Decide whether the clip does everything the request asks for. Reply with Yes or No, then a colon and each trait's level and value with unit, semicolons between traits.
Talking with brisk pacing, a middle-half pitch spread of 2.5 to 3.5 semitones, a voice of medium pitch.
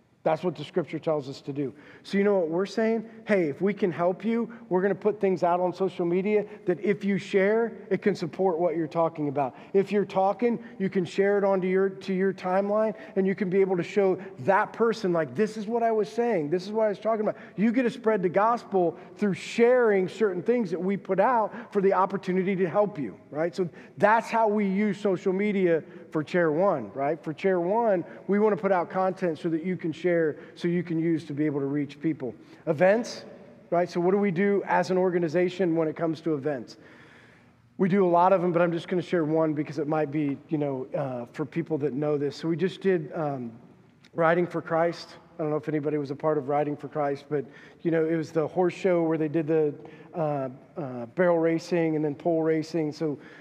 No: fast, 240 wpm; average, 3.9 semitones; medium, 180 Hz